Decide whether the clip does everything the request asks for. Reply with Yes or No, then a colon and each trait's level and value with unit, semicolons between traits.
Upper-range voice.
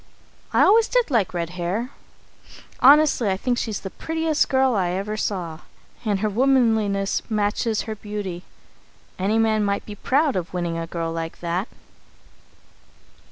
Yes: high, 210 Hz